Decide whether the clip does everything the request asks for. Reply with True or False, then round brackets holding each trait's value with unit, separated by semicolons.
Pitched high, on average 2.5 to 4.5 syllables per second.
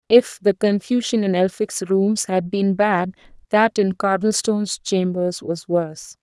True (195 Hz; 4.2 syllables/s)